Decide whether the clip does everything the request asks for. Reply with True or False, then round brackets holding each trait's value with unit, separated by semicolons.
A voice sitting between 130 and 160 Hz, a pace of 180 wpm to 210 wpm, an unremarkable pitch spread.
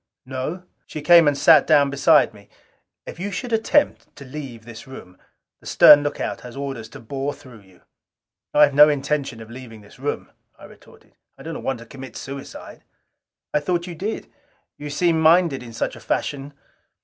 True (140 Hz; 185 wpm; 3.6 semitones)